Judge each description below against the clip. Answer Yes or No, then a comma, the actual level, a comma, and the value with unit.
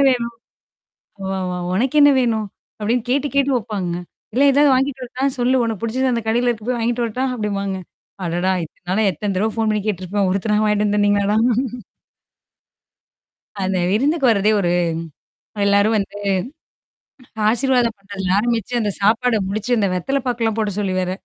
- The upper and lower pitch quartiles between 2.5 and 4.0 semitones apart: Yes, average, 3.5 semitones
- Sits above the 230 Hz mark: No, high, 220 Hz